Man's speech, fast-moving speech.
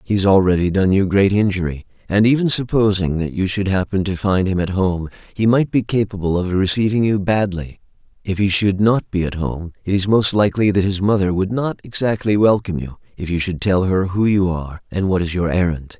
Yes: male; fast, 220 wpm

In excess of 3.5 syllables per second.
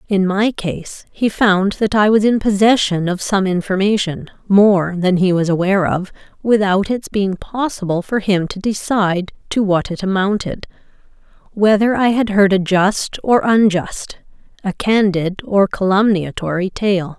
Yes: 4.4 syllables/s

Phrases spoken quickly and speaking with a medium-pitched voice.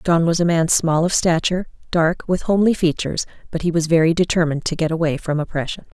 Yes: fast, 210 wpm; medium, 165 Hz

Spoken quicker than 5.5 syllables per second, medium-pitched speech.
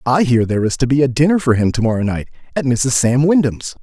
No: 6.2 syllables/s; low, 130 Hz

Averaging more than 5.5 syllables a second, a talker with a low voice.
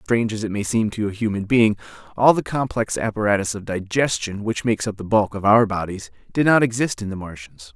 Yes: 5.8 syllables/s; low, 105 Hz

